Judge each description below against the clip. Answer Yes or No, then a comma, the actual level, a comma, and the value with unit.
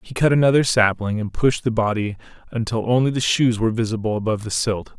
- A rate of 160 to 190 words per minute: No, fast, 205 wpm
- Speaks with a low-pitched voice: Yes, low, 115 Hz